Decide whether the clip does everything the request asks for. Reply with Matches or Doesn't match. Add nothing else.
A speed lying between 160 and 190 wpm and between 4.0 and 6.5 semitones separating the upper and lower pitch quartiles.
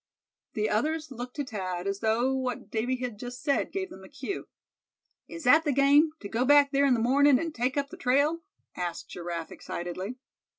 Doesn't match